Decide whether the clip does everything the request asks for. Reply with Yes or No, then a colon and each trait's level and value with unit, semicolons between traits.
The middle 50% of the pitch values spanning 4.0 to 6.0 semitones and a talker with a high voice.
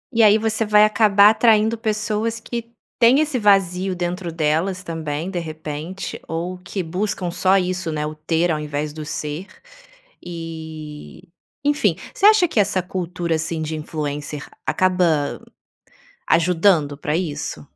No: average, 4.7 semitones; medium, 180 Hz